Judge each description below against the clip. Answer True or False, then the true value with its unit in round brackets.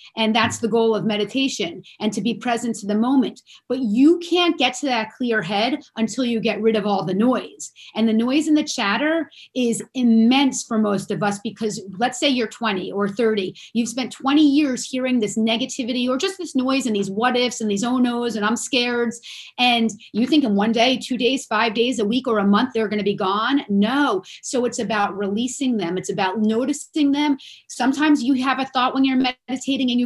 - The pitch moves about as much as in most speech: True (3.3 semitones)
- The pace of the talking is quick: True (220 wpm)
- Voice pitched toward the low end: False (240 Hz)